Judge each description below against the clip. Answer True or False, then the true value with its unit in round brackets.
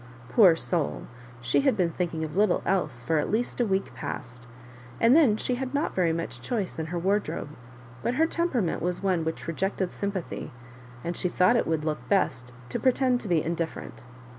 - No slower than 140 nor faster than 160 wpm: False (190 wpm)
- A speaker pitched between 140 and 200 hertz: True (185 Hz)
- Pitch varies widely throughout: True (6.0 semitones)